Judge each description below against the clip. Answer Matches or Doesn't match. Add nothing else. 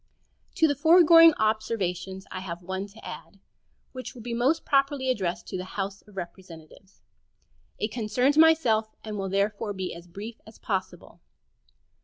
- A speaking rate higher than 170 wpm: Doesn't match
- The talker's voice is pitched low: Doesn't match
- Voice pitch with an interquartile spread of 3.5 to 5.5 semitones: Matches